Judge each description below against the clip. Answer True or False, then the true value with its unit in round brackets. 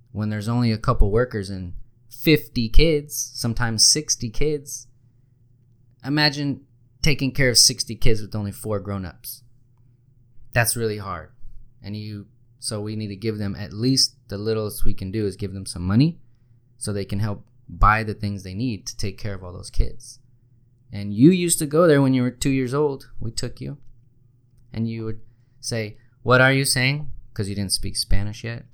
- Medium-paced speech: True (190 wpm)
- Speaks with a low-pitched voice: True (120 Hz)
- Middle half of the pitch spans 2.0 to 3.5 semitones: True (3.1 semitones)